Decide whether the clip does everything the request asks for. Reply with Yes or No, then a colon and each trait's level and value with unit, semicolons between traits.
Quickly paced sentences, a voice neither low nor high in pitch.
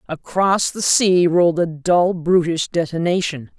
No: slow, 135 wpm; medium, 170 Hz